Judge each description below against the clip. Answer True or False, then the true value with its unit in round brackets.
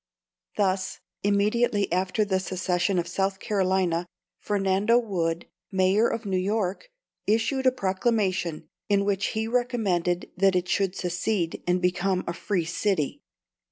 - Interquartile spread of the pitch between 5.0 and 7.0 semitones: False (2.6 semitones)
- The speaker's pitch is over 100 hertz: True (190 Hz)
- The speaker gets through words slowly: True (130 wpm)